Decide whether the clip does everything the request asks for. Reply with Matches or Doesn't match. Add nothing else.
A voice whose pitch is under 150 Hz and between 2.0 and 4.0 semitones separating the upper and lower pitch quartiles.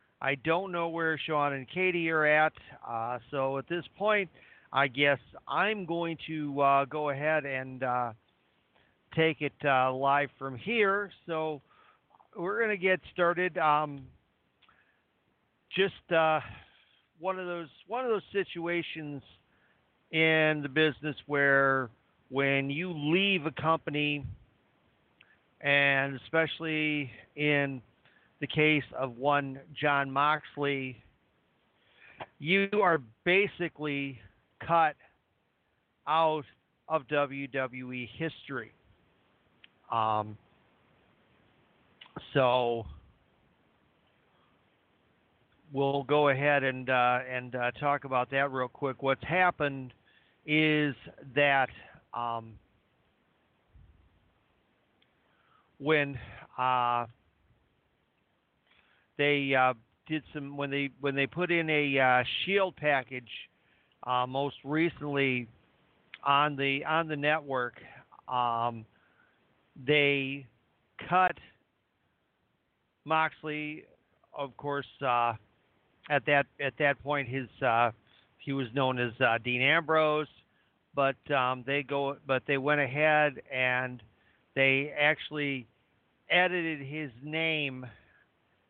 Matches